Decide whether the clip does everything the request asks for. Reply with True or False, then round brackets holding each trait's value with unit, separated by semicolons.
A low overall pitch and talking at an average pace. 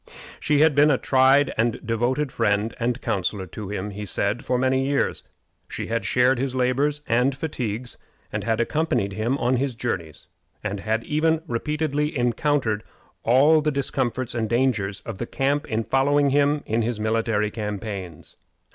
True (125 Hz; 160 wpm)